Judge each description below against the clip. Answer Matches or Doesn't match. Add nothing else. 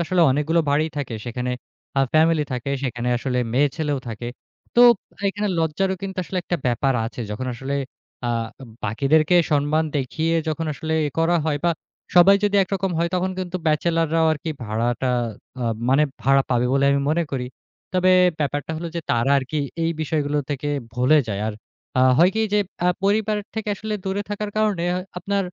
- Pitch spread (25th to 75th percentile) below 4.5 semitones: Doesn't match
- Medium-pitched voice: Matches